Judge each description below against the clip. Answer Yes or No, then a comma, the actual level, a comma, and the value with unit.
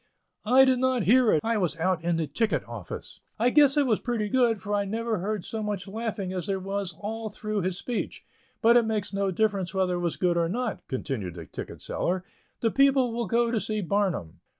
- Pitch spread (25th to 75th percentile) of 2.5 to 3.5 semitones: No, average, 4.1 semitones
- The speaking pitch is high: Yes, high, 210 Hz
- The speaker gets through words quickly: Yes, fast, 220 wpm